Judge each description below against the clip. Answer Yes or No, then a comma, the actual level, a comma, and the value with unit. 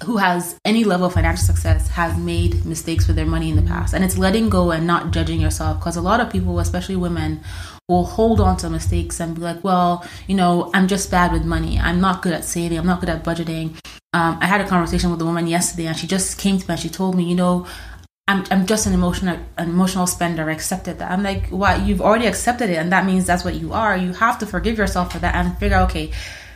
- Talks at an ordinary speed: No, fast, 260 wpm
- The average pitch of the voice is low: No, medium, 170 Hz